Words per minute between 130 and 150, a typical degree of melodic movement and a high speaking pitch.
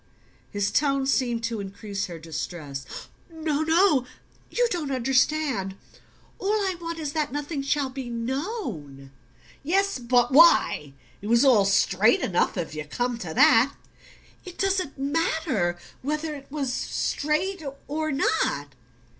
No: slow, 135 wpm; wide, 7.4 semitones; very high, 270 Hz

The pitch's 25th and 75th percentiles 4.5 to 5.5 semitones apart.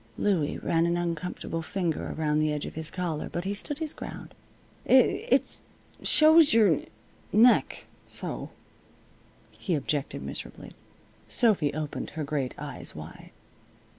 Yes: average, 5.1 semitones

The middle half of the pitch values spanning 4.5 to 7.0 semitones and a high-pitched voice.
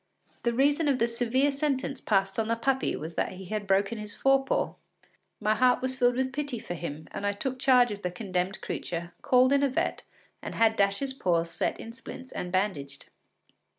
Yes: average, 5.3 semitones; high, 230 Hz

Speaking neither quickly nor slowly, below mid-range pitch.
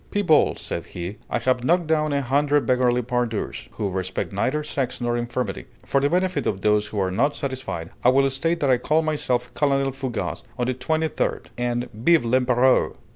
Yes: average, 190 wpm; low, 130 Hz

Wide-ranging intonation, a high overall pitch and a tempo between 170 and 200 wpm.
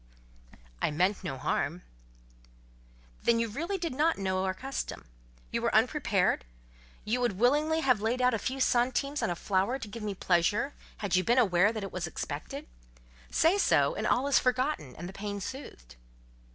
Yes: wide, 6.0 semitones; high, 225 Hz; average, 180 wpm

